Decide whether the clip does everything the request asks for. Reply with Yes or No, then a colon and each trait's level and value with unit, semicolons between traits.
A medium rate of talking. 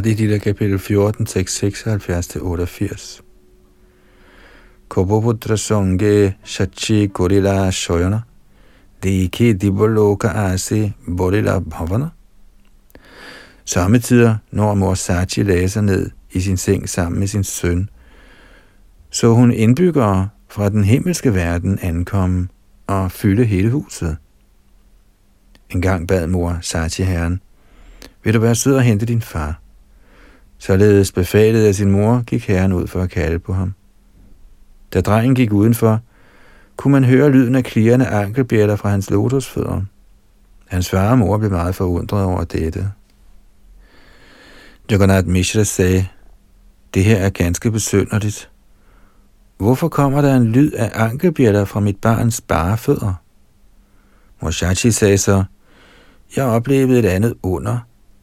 No: slow, 120 wpm